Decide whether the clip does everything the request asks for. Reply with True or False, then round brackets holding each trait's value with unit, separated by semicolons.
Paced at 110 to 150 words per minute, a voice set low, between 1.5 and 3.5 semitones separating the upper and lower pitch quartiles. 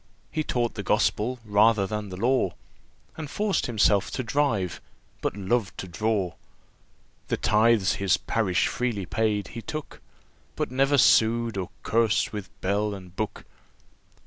True (145 wpm; 110 Hz; 3.2 semitones)